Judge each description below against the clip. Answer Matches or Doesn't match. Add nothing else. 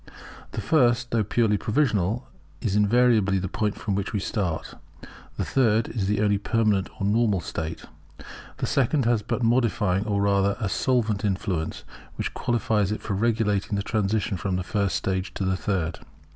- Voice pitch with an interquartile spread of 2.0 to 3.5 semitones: Matches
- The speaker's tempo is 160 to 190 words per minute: Matches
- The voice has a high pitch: Doesn't match